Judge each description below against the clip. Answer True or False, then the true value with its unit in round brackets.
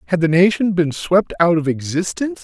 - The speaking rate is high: False (195 wpm)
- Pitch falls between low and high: True (170 Hz)